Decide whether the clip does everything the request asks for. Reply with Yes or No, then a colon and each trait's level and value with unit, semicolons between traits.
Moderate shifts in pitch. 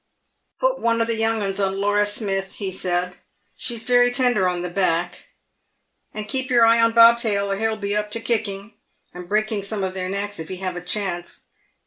Yes: average, 3.1 semitones